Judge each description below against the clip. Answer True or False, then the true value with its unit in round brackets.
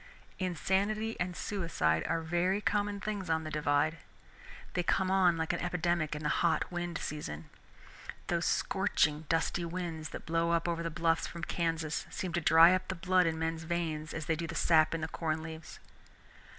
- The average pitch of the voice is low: False (165 Hz)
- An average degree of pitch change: False (1.9 semitones)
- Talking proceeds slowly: False (185 wpm)